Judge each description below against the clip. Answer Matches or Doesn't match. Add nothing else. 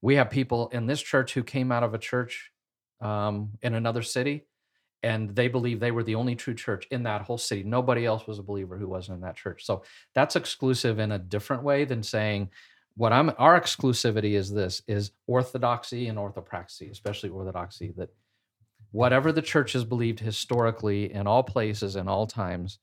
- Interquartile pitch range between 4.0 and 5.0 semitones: Doesn't match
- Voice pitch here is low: Matches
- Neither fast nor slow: Matches